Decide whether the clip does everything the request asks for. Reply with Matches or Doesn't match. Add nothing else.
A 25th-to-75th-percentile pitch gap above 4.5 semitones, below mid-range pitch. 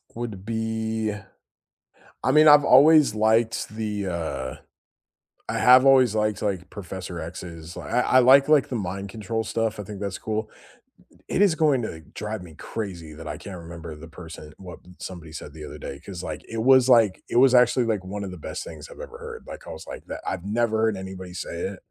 Matches